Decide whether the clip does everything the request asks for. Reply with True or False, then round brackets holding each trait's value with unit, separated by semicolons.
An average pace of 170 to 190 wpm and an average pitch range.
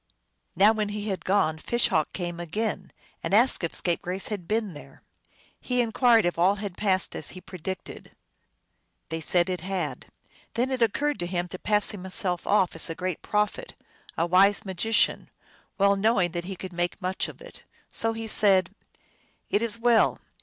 True (180 wpm; 3.7 semitones)